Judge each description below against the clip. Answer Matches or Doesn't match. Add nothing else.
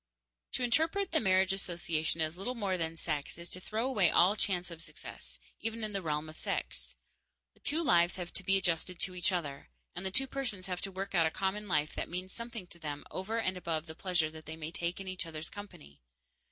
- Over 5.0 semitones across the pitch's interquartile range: Doesn't match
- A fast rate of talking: Matches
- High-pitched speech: Doesn't match